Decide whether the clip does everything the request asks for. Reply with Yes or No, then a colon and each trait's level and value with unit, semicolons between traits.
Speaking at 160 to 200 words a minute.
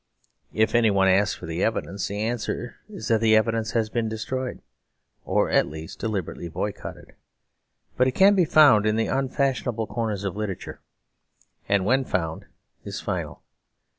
No: average, 150 wpm